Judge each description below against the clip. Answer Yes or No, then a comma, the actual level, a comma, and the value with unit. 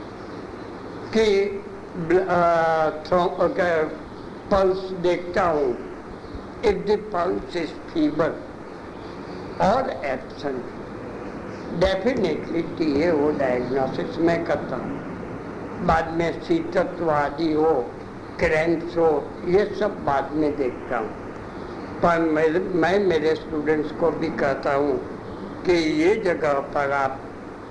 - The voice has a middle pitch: Yes, medium, 170 Hz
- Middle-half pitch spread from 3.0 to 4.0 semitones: Yes, average, 3.7 semitones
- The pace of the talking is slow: Yes, slow, 95 wpm